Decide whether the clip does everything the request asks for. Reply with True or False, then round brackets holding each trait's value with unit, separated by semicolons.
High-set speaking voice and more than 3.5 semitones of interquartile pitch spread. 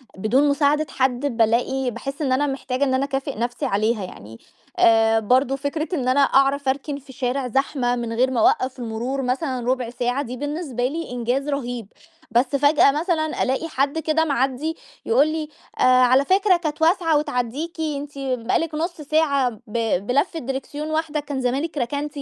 False (270 Hz; 3.2 semitones)